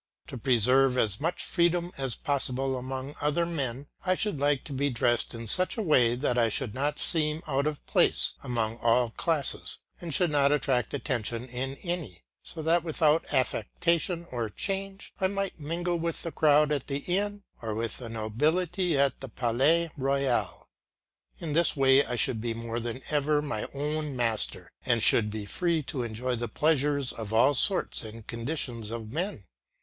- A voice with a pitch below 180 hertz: Yes, medium, 140 Hz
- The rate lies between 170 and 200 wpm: Yes, average, 175 wpm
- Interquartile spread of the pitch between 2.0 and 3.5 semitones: No, average, 5.3 semitones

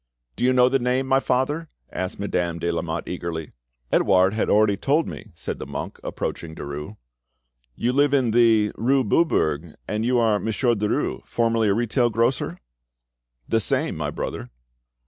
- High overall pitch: No, low, 110 Hz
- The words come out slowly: No, average, 165 wpm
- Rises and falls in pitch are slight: No, wide, 5.4 semitones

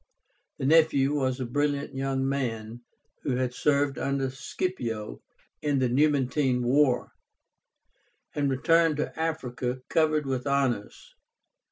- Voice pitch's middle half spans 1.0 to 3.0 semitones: Yes, narrow, 2.6 semitones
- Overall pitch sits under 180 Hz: Yes, low, 135 Hz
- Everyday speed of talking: No, slow, 120 wpm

